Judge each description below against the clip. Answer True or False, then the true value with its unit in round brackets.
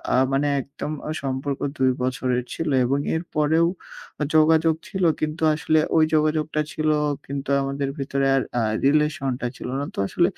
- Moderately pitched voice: True (145 Hz)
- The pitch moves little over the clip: True (2.3 semitones)